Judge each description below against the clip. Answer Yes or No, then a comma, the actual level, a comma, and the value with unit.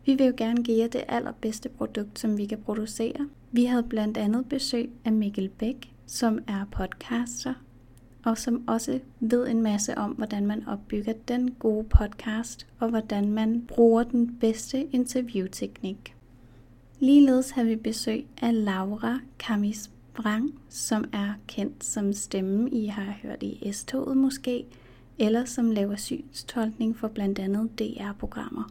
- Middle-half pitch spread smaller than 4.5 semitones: Yes, average, 2.8 semitones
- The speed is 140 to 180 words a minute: Yes, average, 150 wpm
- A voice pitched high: Yes, high, 225 Hz